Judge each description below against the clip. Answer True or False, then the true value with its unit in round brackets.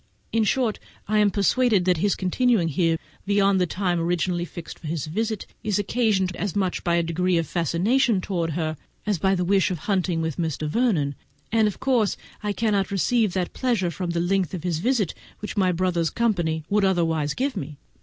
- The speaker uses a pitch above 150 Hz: True (185 Hz)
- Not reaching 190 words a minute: False (195 wpm)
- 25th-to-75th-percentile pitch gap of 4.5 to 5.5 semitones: False (3.7 semitones)